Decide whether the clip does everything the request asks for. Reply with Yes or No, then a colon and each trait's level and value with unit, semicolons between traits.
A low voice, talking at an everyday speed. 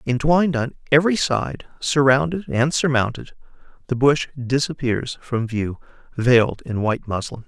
No: low, 130 Hz; slow, 130 wpm